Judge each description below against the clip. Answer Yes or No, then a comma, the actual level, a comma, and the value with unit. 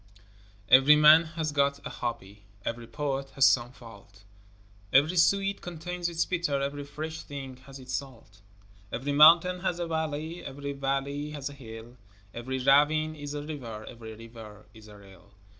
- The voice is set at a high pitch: No, medium, 140 Hz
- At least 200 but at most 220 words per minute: No, average, 160 wpm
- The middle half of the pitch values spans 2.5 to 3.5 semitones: No, average, 4.7 semitones